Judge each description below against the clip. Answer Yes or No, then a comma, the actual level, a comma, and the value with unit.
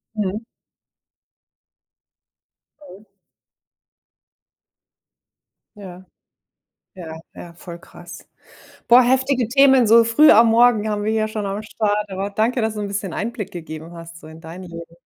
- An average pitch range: Yes, average, 4.6 semitones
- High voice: Yes, high, 205 Hz